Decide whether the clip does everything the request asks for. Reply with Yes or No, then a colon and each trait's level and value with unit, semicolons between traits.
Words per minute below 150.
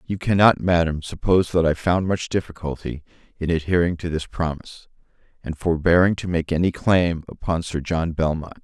No: average, 165 wpm